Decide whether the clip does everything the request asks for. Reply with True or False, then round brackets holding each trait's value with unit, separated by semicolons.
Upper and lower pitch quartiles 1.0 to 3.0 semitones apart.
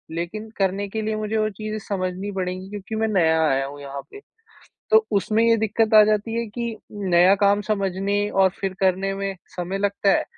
True (2.5 semitones)